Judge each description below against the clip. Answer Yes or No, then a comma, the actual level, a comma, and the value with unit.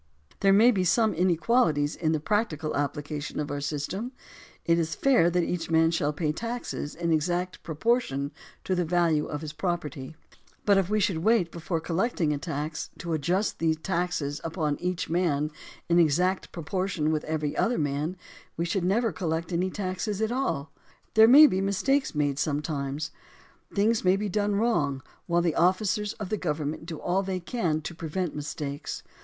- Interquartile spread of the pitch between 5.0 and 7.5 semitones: No, average, 4.2 semitones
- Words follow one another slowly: No, average, 175 wpm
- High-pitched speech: No, medium, 170 Hz